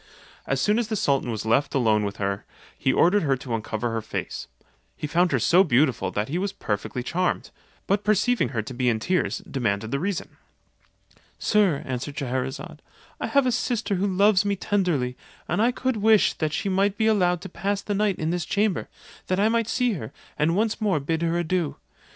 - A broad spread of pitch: Yes, wide, 8.0 semitones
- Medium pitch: Yes, medium, 175 Hz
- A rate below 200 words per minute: No, fast, 205 wpm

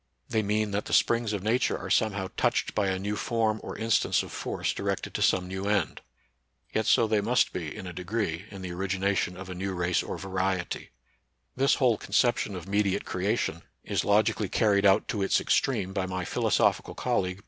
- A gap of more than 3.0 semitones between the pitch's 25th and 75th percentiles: No, narrow, 2.6 semitones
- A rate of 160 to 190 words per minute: No, fast, 205 wpm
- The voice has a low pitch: Yes, low, 100 Hz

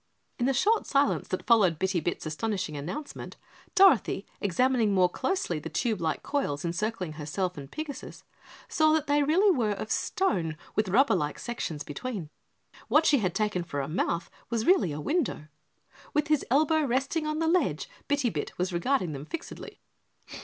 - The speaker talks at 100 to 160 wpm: No, average, 170 wpm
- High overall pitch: Yes, high, 220 Hz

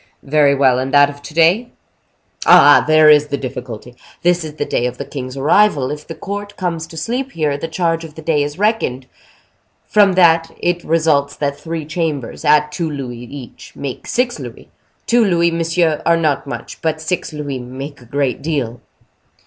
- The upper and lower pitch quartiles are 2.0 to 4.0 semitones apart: Yes, average, 3.1 semitones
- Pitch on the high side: No, medium, 155 Hz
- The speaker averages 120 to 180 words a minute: No, average, 190 wpm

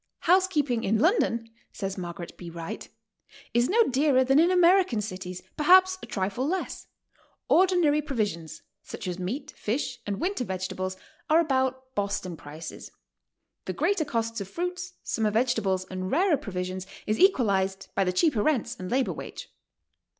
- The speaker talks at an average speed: Yes, average, 150 wpm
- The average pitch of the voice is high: Yes, high, 235 Hz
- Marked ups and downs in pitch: Yes, wide, 8.5 semitones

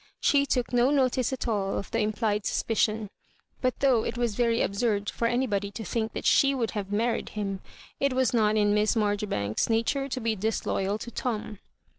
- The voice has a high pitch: Yes, high, 225 Hz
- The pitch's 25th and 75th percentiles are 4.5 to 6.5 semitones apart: No, average, 2.9 semitones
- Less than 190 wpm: No, average, 195 wpm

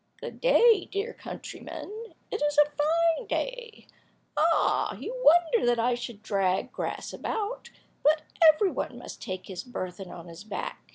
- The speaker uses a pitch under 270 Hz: No, very high, 300 Hz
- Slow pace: No, average, 155 wpm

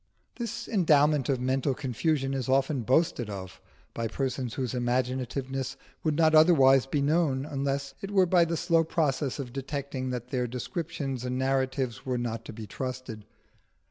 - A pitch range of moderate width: Yes, average, 3.0 semitones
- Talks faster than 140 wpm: Yes, average, 160 wpm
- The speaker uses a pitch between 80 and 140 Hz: Yes, low, 135 Hz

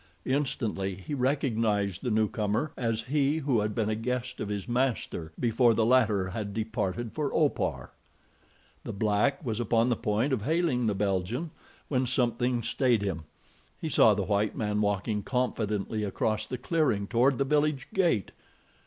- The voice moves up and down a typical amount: Yes, average, 3.7 semitones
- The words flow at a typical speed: Yes, average, 160 wpm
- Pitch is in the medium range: No, low, 115 Hz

